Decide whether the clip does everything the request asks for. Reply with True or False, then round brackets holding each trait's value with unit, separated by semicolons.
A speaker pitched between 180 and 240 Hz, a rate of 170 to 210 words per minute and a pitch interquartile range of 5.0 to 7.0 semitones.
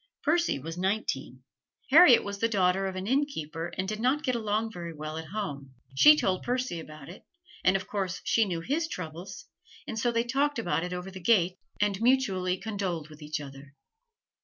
True (190 Hz; 190 wpm; 5.6 semitones)